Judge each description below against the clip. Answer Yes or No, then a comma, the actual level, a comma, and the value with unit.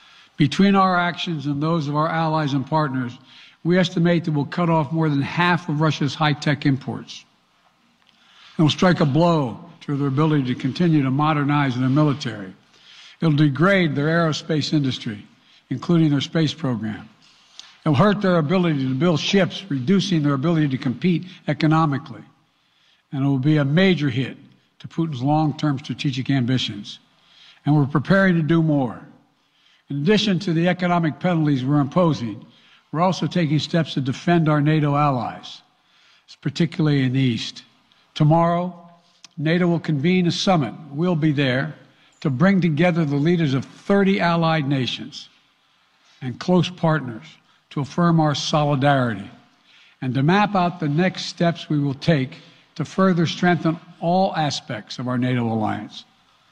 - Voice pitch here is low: No, medium, 155 Hz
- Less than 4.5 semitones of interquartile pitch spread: Yes, average, 3.6 semitones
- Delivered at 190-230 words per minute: No, average, 155 wpm